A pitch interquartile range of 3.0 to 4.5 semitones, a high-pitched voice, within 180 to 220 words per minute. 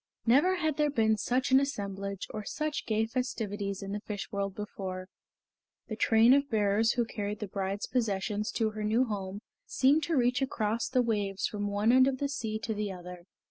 Yes: average, 3.9 semitones; high, 215 Hz; average, 195 wpm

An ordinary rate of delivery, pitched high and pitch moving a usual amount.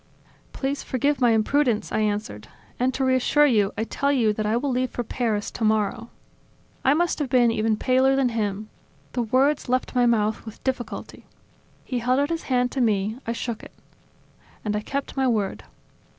Yes: average, 185 wpm; high, 245 Hz; average, 3.4 semitones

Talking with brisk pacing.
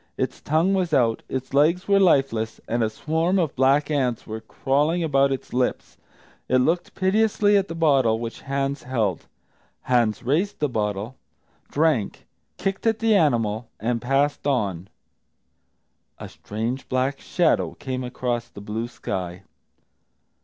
No: average, 145 wpm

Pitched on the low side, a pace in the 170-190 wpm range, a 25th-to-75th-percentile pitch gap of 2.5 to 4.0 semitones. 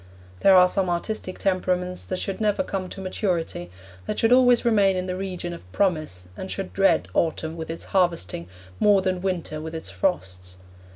No: medium, 185 Hz; average, 180 wpm; average, 2.9 semitones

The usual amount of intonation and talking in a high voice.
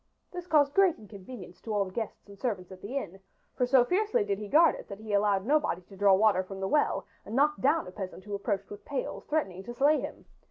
No: wide, 6.7 semitones; high, 215 Hz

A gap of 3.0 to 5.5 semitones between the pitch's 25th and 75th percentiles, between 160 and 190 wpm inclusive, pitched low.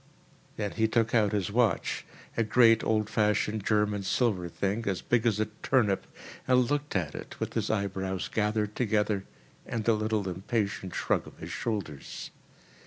No: narrow, 2.4 semitones; average, 165 wpm; low, 105 Hz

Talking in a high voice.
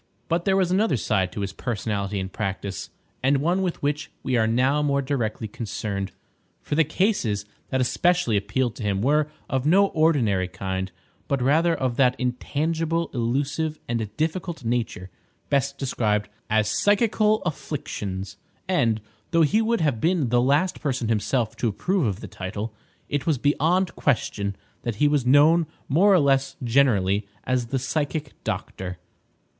No: low, 130 Hz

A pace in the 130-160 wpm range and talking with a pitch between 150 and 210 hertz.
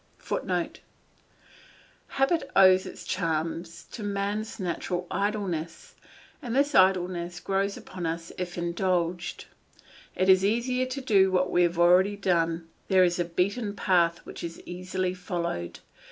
Yes: slow, 135 wpm; medium, 185 Hz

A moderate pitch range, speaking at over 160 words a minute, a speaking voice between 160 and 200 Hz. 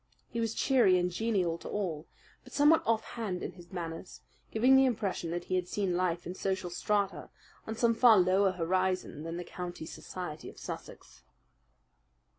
Yes: average, 4.0 semitones; average, 170 wpm; medium, 185 Hz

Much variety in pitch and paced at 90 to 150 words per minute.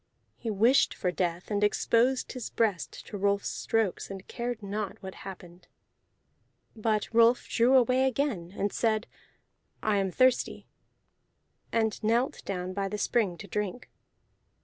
No: average, 3.3 semitones; average, 140 wpm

